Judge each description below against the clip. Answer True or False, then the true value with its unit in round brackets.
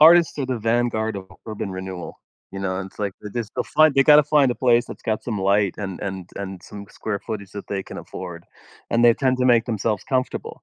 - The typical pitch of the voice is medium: False (110 Hz)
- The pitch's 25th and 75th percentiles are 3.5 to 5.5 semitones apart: True (4.1 semitones)